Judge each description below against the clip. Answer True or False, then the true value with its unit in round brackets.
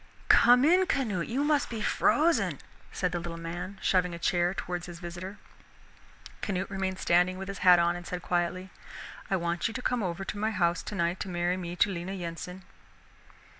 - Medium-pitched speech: True (180 Hz)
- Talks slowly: False (190 wpm)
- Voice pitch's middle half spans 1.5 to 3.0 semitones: True (2.5 semitones)